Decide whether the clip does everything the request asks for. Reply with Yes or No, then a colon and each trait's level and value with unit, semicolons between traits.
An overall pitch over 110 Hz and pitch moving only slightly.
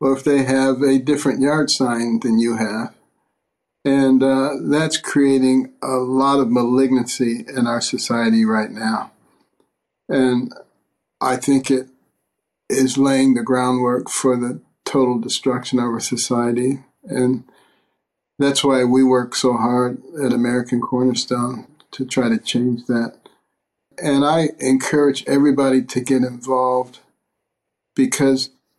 Yes: low, 130 Hz; narrow, 1.6 semitones